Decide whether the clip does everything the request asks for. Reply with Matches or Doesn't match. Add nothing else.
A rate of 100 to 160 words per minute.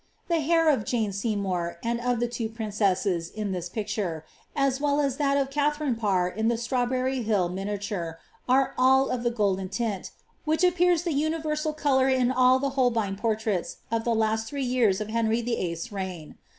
Doesn't match